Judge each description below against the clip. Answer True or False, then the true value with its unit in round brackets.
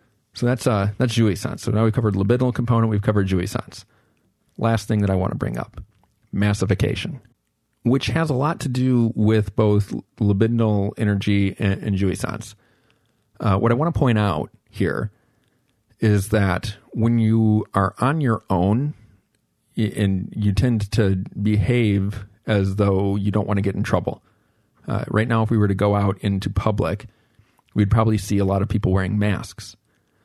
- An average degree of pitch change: False (2.3 semitones)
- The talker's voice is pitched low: True (110 Hz)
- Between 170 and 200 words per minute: True (175 wpm)